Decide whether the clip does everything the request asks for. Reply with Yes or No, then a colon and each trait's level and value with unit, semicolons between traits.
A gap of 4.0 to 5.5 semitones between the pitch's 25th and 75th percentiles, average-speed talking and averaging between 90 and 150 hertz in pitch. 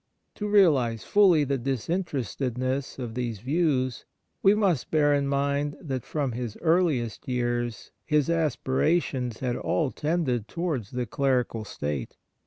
No: average, 4.6 semitones; slow, 130 wpm; low, 135 Hz